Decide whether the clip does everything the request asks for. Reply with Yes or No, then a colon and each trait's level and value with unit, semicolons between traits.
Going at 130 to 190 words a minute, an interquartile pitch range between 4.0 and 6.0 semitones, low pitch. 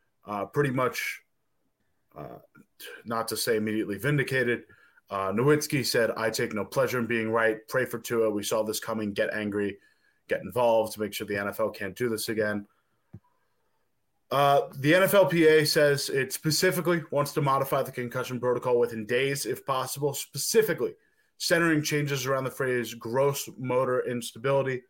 Yes: average, 155 wpm; average, 4.3 semitones; low, 125 Hz